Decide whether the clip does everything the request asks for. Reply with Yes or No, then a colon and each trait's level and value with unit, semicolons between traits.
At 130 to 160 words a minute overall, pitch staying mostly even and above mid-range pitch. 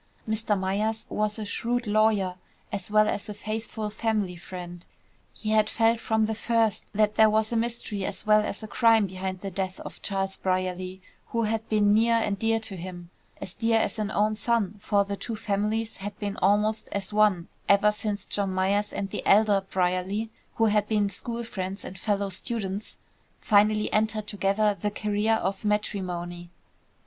No: average, 175 wpm; narrow, 2.1 semitones; high, 210 Hz